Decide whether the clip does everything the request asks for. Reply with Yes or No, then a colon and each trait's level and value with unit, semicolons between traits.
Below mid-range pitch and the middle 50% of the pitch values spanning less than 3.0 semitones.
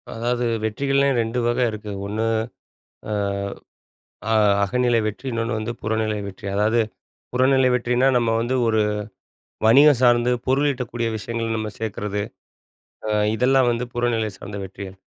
Yes: low, 115 Hz; narrow, 2.5 semitones